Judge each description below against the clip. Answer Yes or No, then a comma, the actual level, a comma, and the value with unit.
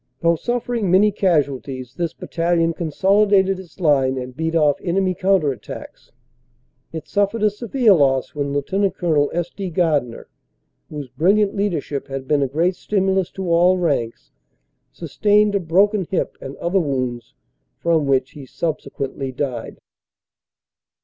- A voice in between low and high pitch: Yes, medium, 170 Hz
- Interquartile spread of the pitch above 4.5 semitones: Yes, wide, 5.4 semitones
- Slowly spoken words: No, average, 145 wpm